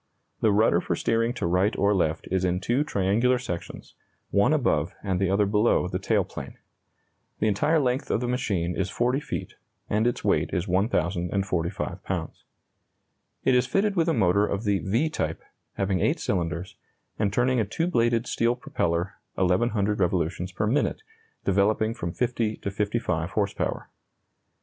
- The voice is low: Yes, low, 100 Hz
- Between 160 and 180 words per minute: Yes, average, 165 wpm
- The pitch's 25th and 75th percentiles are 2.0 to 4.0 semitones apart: No, average, 4.4 semitones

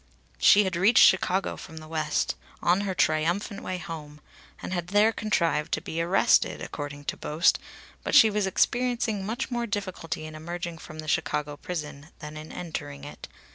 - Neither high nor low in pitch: Yes, medium, 170 Hz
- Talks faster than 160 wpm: Yes, average, 175 wpm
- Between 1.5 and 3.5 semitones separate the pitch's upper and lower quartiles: No, average, 4.2 semitones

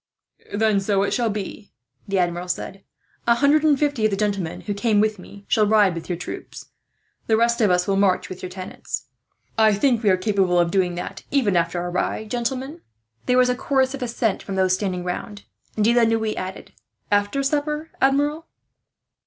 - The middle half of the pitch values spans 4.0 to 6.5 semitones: Yes, average, 4.5 semitones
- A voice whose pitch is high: Yes, high, 210 Hz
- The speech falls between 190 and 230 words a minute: Yes, average, 200 wpm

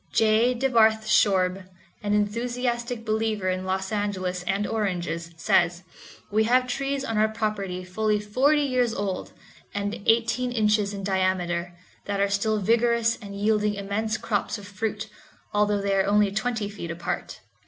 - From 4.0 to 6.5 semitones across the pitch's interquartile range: No, narrow, 2.5 semitones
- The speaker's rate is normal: Yes, average, 150 wpm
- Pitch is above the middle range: Yes, high, 210 Hz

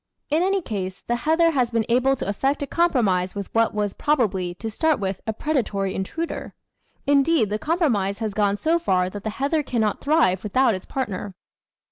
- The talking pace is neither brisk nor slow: Yes, average, 185 wpm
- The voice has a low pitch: No, high, 230 Hz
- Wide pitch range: Yes, wide, 6.7 semitones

